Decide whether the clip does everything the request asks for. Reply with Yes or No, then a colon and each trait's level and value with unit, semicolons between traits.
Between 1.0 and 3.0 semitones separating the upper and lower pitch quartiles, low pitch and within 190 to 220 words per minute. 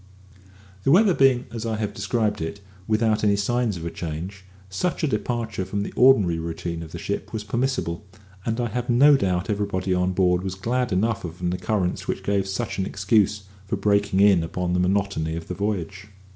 No: average, 3.8 semitones; low, 100 Hz; average, 200 wpm